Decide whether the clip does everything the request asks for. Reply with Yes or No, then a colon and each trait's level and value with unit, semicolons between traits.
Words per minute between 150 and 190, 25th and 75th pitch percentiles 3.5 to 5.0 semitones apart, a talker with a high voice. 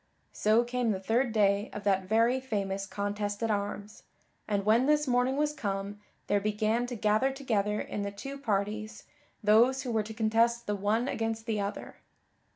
No: average, 175 wpm; average, 2.8 semitones; high, 215 Hz